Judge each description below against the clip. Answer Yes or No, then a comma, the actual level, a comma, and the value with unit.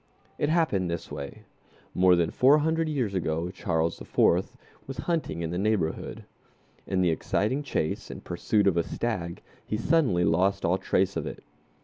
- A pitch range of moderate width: No, wide, 7.4 semitones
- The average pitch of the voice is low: Yes, very low, 95 Hz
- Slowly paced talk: No, average, 165 wpm